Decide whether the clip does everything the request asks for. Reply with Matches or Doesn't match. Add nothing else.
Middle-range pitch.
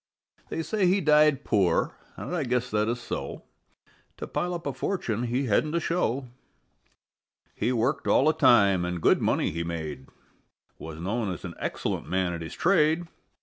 Doesn't match